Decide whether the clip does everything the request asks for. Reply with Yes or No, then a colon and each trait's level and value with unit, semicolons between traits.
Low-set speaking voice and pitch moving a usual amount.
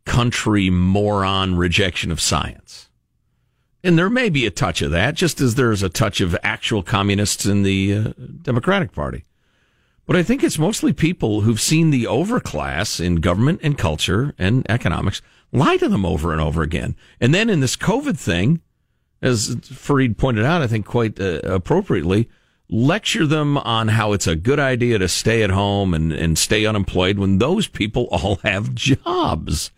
No: low, 105 Hz; wide, 6.1 semitones